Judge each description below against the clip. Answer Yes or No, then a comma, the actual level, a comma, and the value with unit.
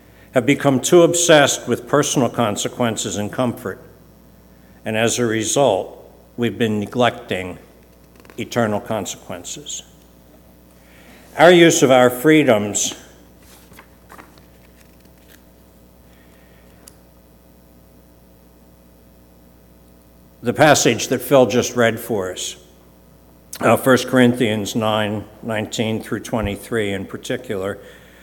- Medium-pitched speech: No, very low, 95 Hz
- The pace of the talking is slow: Yes, slow, 85 wpm